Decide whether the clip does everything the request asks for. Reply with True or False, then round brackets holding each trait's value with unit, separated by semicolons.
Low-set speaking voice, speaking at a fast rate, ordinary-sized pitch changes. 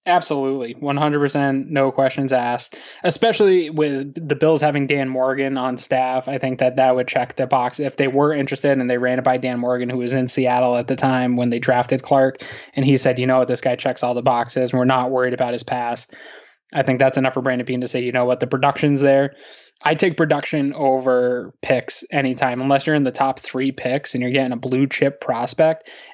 False (130 Hz; 225 wpm; 1.9 semitones)